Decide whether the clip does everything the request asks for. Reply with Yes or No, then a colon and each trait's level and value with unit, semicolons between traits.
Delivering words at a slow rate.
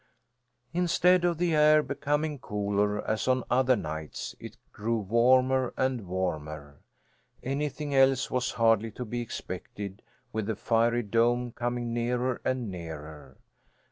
Yes: slow, 130 wpm